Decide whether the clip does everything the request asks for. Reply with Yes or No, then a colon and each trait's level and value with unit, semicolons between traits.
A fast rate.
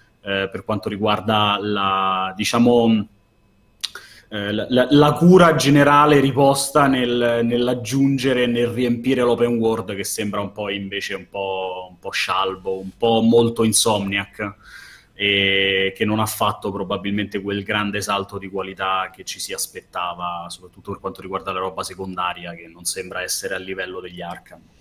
No: average, 150 wpm